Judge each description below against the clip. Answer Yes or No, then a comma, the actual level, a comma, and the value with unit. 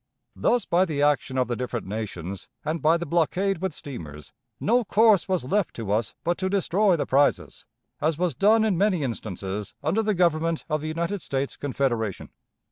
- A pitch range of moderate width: No, wide, 7.0 semitones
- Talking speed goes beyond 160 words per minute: Yes, average, 185 wpm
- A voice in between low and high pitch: Yes, medium, 155 Hz